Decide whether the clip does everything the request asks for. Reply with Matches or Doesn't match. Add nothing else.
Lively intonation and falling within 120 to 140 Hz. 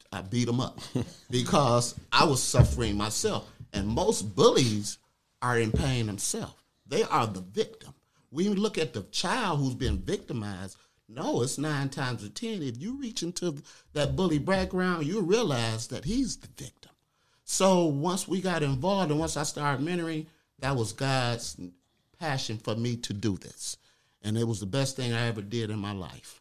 Matches